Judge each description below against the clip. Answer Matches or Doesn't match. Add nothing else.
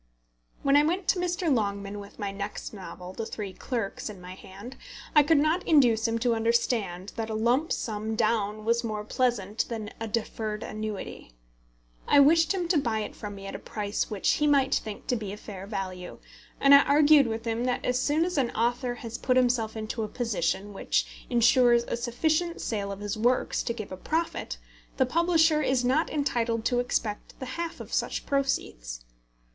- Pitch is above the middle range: Matches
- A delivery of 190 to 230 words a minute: Matches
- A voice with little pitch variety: Doesn't match